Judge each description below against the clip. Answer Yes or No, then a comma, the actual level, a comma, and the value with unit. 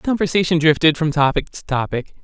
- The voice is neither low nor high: Yes, medium, 160 Hz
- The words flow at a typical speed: Yes, average, 190 wpm